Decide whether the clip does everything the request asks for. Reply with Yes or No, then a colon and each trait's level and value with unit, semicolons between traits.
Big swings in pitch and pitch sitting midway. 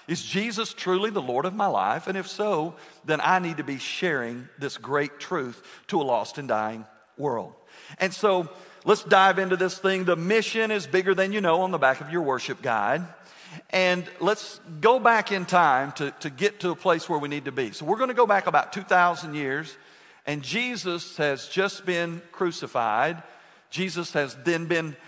No: average, 4.5 semitones; medium, 175 Hz